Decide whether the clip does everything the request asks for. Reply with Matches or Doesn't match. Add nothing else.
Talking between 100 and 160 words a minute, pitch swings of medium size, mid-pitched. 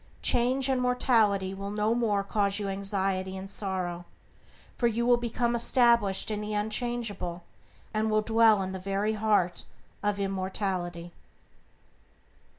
Doesn't match